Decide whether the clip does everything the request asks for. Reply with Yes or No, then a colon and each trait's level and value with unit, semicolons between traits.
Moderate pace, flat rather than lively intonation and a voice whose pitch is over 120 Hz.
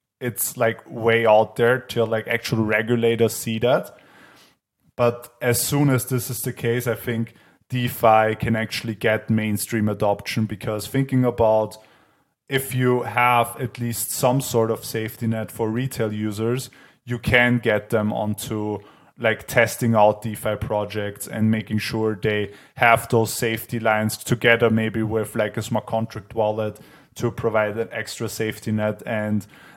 No: average, 155 wpm; narrow, 1.9 semitones; low, 115 Hz